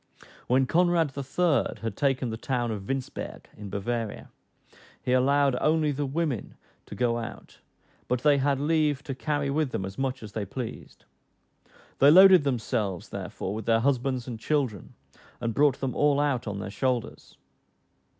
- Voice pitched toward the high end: No, low, 130 Hz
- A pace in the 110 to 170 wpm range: Yes, average, 160 wpm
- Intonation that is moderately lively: Yes, average, 3.8 semitones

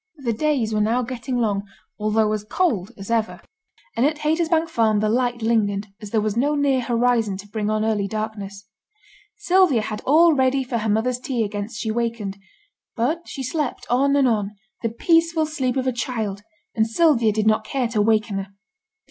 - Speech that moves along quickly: No, average, 190 wpm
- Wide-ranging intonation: No, average, 3.7 semitones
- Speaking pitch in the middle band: No, high, 230 Hz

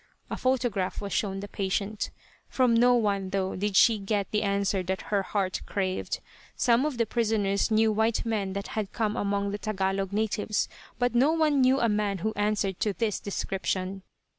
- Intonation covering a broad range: No, narrow, 2.4 semitones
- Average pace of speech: Yes, average, 185 wpm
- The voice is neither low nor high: No, high, 205 Hz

